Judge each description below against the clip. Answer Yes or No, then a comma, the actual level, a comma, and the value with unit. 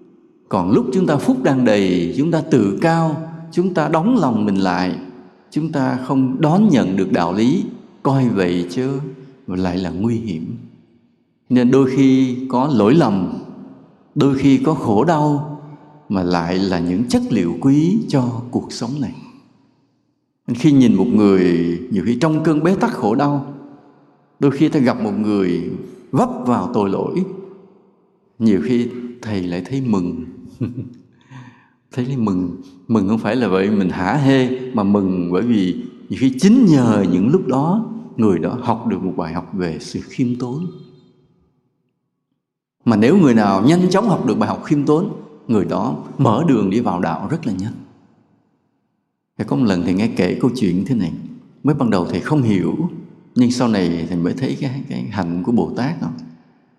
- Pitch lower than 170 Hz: Yes, low, 135 Hz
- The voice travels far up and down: Yes, wide, 7.2 semitones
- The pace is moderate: Yes, average, 180 wpm